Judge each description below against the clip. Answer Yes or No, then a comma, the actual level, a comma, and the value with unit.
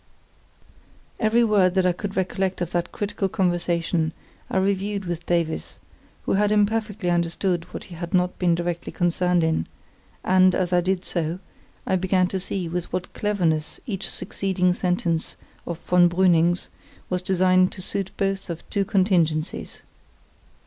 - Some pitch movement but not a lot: No, narrow, 1.9 semitones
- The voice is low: No, medium, 180 Hz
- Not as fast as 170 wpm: Yes, average, 150 wpm